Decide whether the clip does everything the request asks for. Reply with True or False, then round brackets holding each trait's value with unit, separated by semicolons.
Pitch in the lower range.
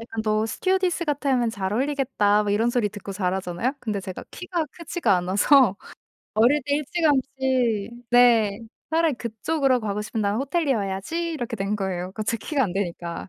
False (230 Hz)